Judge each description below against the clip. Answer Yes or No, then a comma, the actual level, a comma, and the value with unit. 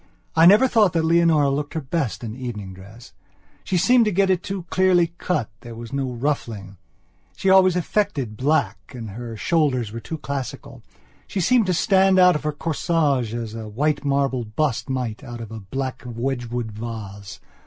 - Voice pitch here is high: No, low, 135 Hz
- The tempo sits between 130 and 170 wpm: No, average, 180 wpm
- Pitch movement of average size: No, wide, 6.6 semitones